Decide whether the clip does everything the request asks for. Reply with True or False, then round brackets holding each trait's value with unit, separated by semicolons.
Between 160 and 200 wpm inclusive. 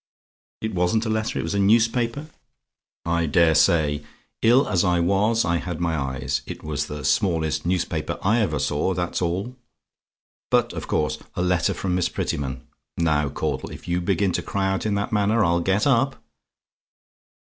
True (170 wpm)